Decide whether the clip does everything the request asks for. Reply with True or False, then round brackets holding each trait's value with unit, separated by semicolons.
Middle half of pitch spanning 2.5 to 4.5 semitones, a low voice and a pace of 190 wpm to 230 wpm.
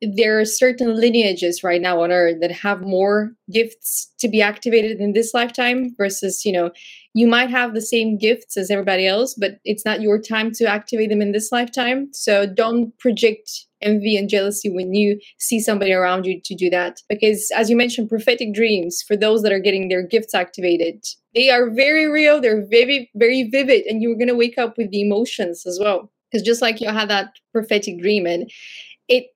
False (2.8 semitones; 215 Hz; 200 wpm)